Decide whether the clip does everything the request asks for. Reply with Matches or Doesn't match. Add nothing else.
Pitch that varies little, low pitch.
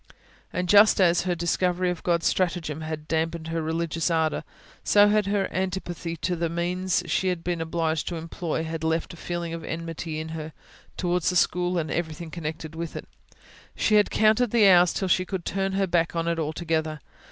Doesn't match